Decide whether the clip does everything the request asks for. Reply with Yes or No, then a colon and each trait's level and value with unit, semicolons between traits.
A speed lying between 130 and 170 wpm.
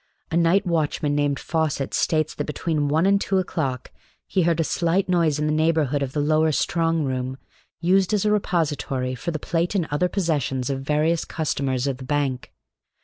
No: average, 190 wpm